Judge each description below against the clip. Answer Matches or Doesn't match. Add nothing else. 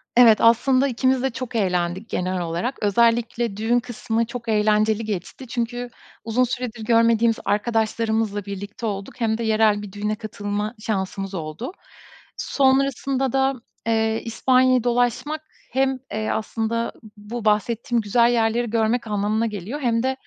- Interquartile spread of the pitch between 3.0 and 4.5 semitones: Doesn't match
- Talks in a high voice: Matches